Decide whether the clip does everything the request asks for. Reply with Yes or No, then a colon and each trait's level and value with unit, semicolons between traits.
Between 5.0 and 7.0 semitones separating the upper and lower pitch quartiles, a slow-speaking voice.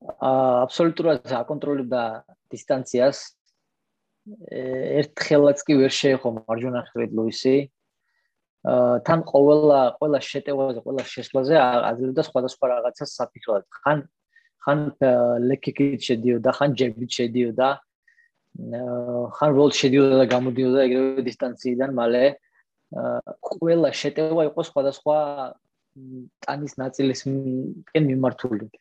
No: narrow, 2.5 semitones; slow, 85 wpm